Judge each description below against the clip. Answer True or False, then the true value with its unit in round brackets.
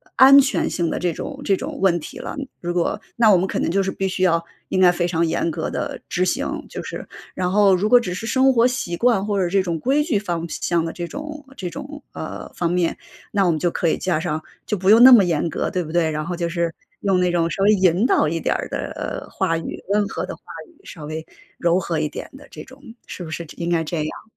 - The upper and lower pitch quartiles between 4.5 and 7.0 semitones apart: False (3.7 semitones)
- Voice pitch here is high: False (180 Hz)